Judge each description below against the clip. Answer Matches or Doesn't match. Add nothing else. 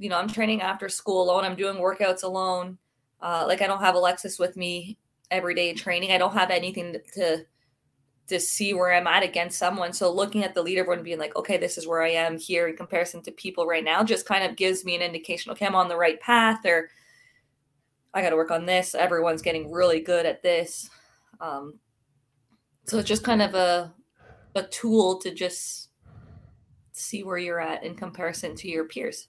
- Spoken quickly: Matches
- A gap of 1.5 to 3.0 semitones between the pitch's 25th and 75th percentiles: Matches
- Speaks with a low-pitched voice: Doesn't match